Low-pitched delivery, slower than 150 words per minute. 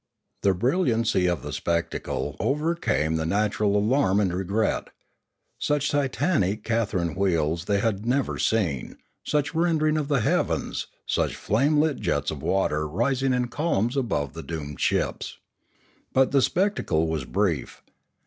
Yes: low, 110 Hz; average, 140 wpm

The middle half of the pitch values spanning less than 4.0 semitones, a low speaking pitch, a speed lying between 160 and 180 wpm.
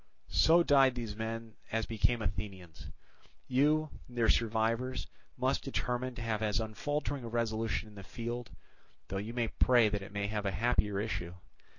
Yes: average, 2.7 semitones; low, 115 Hz; average, 165 wpm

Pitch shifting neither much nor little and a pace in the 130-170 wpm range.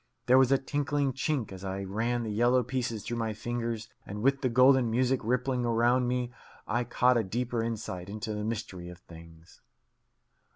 No: average, 3.0 semitones; average, 180 wpm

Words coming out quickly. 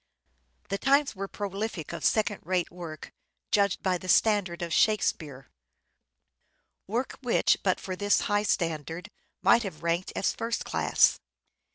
No: average, 140 wpm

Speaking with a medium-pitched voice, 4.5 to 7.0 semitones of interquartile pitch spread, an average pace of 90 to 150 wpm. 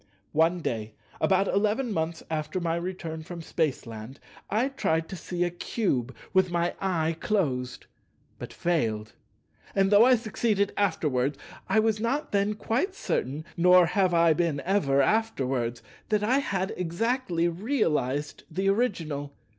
Yes: medium, 175 Hz; average, 5.2 semitones; average, 140 wpm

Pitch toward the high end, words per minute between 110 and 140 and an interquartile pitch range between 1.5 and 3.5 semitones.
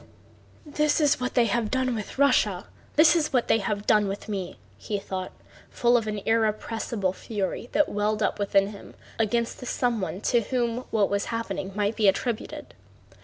No: high, 220 Hz; average, 175 wpm; average, 3.2 semitones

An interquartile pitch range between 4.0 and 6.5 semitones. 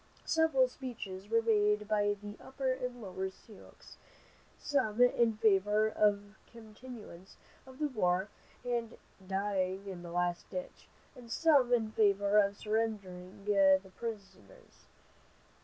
No: average, 3.4 semitones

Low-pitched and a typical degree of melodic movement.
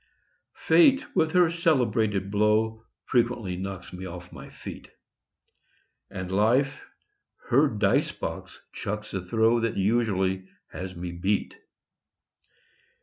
Yes: low, 105 Hz; average, 4.1 semitones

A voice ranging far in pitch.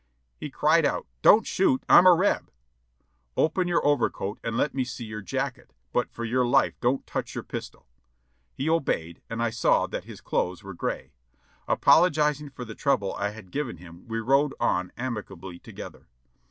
Yes: wide, 6.6 semitones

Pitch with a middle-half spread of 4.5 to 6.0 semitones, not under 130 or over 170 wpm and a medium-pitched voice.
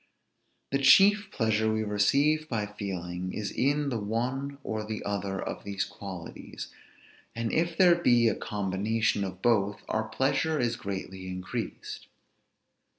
No: average, 5.3 semitones; average, 140 wpm; low, 110 Hz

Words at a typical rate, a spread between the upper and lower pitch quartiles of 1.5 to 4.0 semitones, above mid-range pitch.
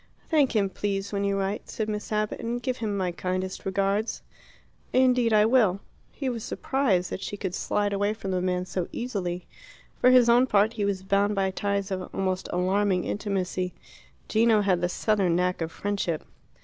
Yes: average, 185 wpm; average, 2.7 semitones; high, 200 Hz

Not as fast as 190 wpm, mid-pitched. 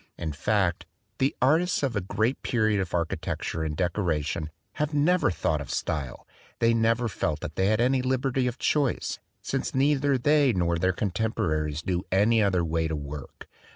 No: average, 170 wpm; low, 105 Hz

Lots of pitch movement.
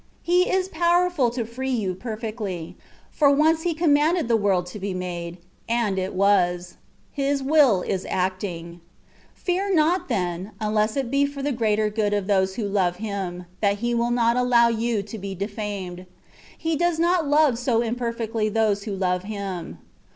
Yes: wide, 6.3 semitones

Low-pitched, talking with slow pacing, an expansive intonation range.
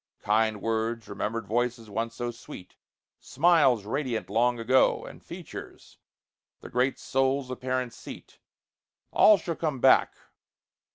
No: low, 120 Hz; slow, 120 wpm; average, 2.7 semitones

